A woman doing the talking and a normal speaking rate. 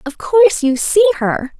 Yes: female; average, 190 wpm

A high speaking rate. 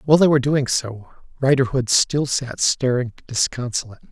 No: average, 145 wpm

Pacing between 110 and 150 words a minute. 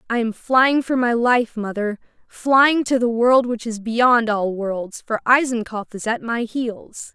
No: average, 185 wpm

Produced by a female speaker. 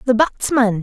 Yes: female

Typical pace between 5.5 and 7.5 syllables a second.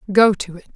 Yes: 7.1 syllables/s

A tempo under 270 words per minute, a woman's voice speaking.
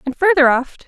Yes: fast, 205 wpm; female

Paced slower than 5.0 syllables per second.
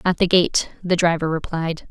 Yes: 4.7 syllables/s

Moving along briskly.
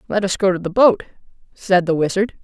Yes: fast, 220 wpm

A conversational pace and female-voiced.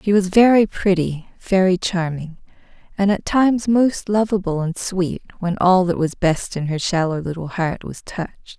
Yes: average, 175 wpm; female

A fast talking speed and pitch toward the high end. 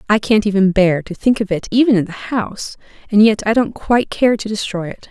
Yes: fast, 245 wpm; high, 210 Hz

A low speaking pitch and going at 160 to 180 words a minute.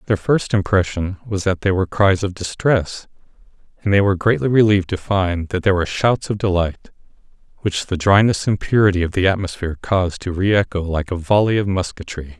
No: very low, 95 Hz; average, 195 wpm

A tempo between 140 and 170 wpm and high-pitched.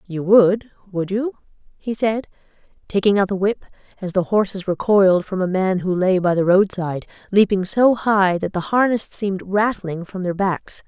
No: average, 180 wpm; high, 195 Hz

